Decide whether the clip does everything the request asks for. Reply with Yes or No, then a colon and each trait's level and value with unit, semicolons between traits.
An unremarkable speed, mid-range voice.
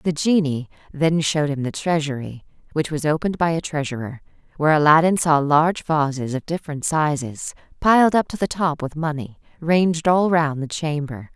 Yes: average, 175 wpm; medium, 155 Hz